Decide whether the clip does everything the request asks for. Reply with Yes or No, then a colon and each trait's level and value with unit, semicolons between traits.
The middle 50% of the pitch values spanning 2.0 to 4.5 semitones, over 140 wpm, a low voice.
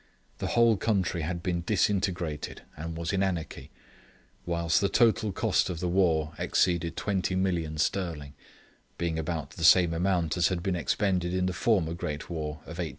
Yes: narrow, 2.4 semitones; average, 175 wpm; very low, 85 Hz